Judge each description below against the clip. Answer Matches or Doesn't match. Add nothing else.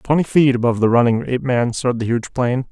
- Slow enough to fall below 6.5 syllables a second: Doesn't match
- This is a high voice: Doesn't match